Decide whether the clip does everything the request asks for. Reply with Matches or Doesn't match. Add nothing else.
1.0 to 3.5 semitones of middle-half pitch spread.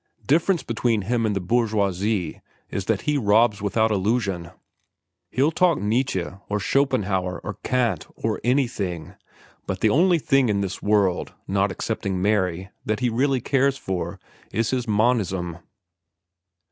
Doesn't match